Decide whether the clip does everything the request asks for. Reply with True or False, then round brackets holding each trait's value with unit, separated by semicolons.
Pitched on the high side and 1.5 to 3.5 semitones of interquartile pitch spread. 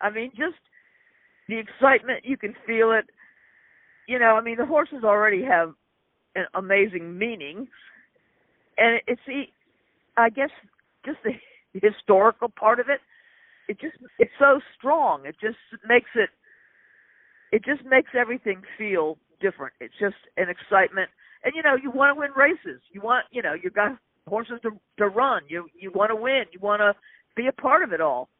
False (240 Hz; 5.3 semitones)